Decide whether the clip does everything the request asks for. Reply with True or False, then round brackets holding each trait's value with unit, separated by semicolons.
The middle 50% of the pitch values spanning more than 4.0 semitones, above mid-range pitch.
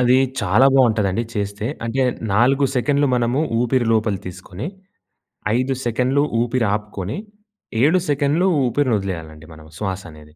False (5.2 semitones; 115 Hz)